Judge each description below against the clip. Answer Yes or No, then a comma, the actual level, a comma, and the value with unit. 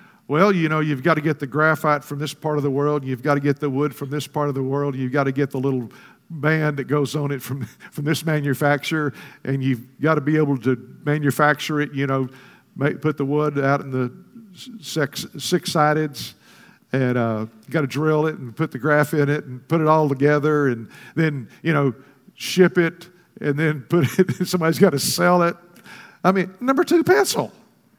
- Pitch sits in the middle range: Yes, medium, 150 Hz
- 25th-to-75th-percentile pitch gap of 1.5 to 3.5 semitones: Yes, narrow, 2.6 semitones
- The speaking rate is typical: No, fast, 215 wpm